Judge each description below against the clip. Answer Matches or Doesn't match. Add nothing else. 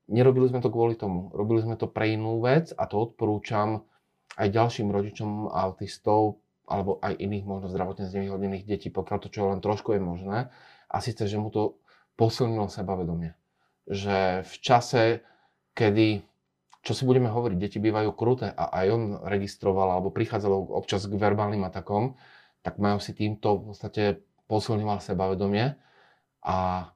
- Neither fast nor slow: Matches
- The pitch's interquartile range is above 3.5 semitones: Doesn't match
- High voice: Doesn't match